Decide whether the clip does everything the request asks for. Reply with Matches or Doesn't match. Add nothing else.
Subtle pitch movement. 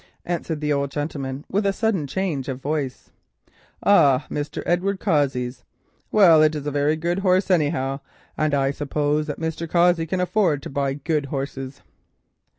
Doesn't match